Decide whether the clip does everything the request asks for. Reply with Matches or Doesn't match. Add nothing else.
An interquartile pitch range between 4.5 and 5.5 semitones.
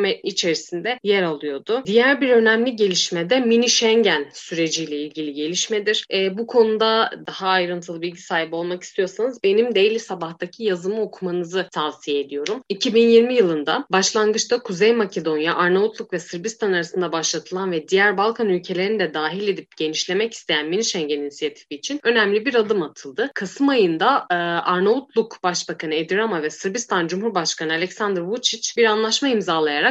Matches